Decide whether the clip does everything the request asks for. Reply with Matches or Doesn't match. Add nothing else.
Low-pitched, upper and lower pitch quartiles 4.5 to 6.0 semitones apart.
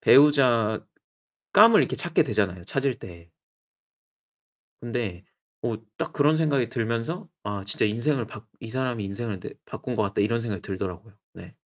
Doesn't match